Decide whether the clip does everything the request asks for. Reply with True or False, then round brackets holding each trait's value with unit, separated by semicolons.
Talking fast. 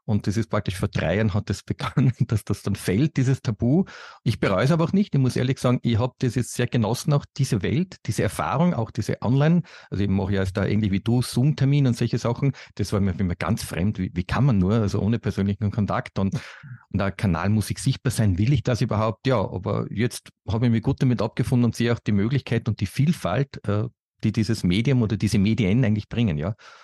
True (240 wpm)